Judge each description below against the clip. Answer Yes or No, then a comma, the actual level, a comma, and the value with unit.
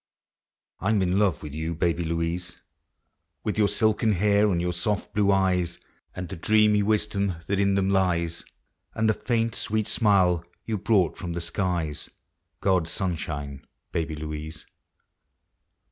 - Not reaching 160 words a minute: Yes, average, 150 wpm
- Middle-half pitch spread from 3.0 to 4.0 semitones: Yes, average, 3.7 semitones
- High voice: No, very low, 95 Hz